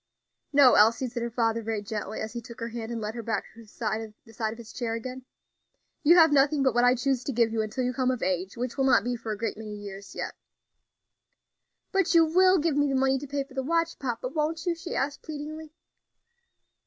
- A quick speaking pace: Yes, fast, 235 wpm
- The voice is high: Yes, high, 245 Hz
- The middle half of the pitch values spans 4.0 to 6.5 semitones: Yes, average, 4.3 semitones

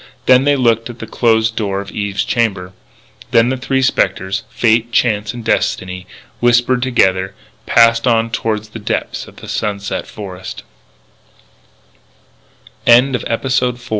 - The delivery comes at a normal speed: No, slow, 125 wpm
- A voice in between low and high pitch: No, low, 115 Hz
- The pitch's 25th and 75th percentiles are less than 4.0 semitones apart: Yes, average, 2.9 semitones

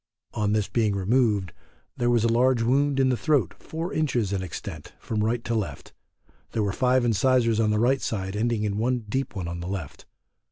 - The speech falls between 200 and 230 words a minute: Yes, fast, 205 wpm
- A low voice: Yes, low, 115 Hz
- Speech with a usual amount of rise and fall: Yes, average, 3.6 semitones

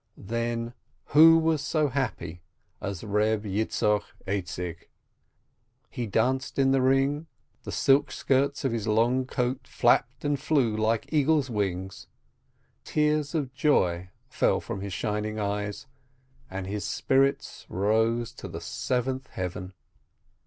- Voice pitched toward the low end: Yes, low, 115 Hz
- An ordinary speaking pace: No, slow, 125 wpm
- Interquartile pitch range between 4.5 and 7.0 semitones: Yes, average, 4.9 semitones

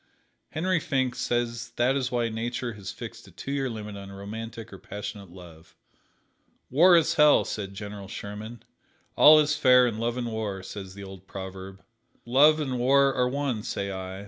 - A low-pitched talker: Yes, low, 115 Hz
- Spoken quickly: No, average, 175 wpm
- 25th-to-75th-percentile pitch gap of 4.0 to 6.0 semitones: Yes, average, 4.8 semitones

